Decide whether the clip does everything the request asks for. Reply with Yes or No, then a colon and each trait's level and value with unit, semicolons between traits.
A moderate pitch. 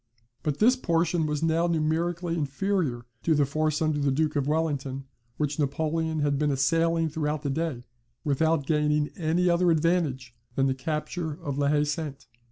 Yes: medium, 155 Hz